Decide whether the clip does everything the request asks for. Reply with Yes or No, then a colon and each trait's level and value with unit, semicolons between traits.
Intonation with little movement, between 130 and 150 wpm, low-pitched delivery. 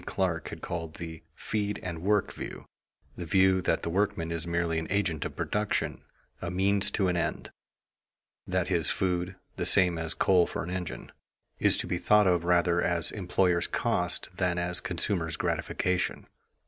No: narrow, 1.9 semitones; average, 170 wpm; very low, 90 Hz